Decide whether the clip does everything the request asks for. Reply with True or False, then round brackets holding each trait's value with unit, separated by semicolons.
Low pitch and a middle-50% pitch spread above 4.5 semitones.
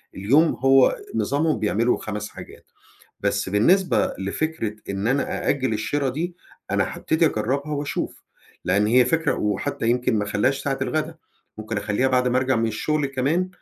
True (130 Hz; 5.3 semitones)